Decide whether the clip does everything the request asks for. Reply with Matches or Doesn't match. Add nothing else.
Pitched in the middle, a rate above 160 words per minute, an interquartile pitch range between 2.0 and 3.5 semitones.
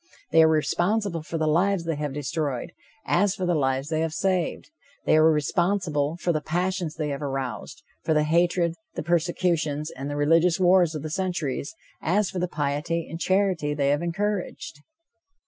Matches